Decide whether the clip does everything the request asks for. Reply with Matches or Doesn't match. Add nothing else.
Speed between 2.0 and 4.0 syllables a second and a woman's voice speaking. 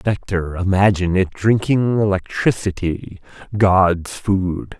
Doesn't match